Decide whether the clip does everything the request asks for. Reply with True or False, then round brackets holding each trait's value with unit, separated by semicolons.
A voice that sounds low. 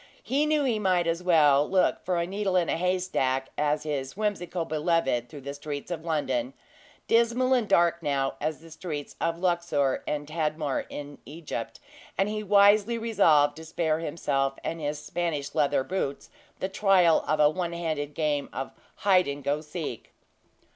False (160 Hz)